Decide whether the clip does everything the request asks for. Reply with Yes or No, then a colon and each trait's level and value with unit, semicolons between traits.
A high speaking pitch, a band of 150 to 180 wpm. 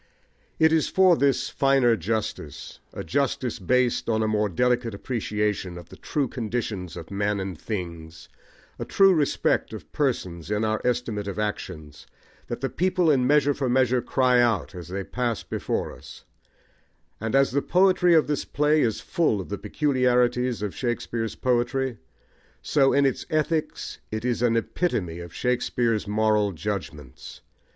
No: low, 120 Hz; average, 160 wpm